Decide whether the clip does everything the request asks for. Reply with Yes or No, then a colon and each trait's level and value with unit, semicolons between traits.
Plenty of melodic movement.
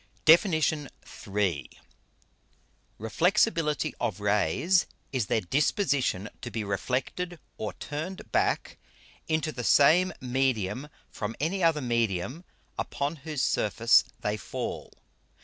Yes: wide, 6.8 semitones